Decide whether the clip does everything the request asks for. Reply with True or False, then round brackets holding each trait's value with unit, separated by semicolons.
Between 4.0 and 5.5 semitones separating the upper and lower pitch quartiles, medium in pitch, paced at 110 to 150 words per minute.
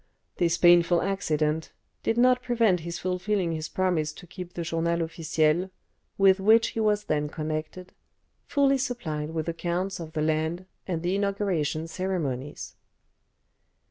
False (3.6 semitones; 175 Hz; 140 wpm)